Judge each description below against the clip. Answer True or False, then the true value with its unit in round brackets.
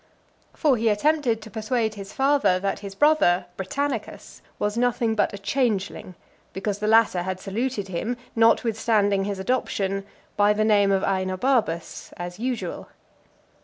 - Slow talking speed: False (145 wpm)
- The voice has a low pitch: False (210 Hz)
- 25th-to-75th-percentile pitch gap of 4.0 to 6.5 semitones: False (3.6 semitones)